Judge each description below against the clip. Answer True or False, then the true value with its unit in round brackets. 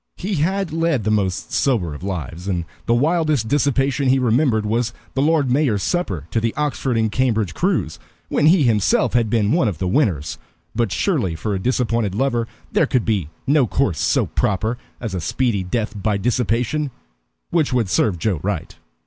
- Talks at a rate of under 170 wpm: False (185 wpm)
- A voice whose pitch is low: True (115 Hz)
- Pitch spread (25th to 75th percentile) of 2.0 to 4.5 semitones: False (5.5 semitones)